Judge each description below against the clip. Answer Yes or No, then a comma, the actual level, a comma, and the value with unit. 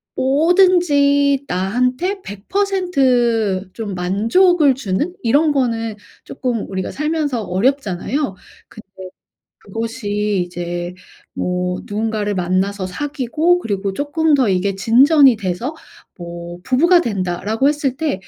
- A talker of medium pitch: No, high, 230 Hz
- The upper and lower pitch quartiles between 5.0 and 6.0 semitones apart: No, wide, 7.1 semitones